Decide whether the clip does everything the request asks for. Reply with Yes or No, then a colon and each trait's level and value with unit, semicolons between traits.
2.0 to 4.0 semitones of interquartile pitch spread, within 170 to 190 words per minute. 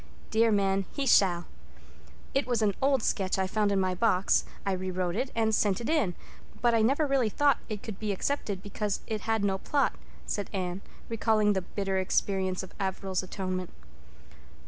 Yes: average, 3.2 semitones; average, 180 wpm